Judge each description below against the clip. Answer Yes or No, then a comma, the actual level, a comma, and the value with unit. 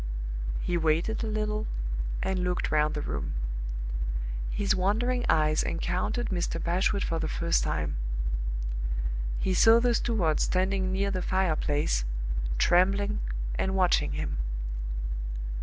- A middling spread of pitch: Yes, average, 4.1 semitones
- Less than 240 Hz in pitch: Yes, medium, 185 Hz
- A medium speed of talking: No, slow, 125 wpm